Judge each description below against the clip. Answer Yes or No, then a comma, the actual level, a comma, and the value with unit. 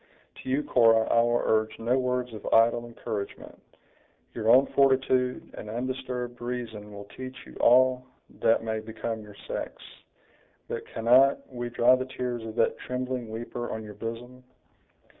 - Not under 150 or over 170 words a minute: Yes, average, 155 wpm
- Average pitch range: No, narrow, 2.1 semitones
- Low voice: Yes, low, 120 Hz